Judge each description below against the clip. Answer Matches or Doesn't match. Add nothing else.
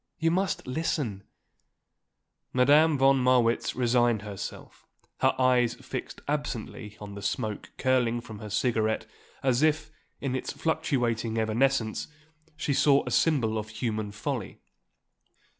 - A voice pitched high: Doesn't match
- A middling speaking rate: Doesn't match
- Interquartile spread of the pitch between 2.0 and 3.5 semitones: Doesn't match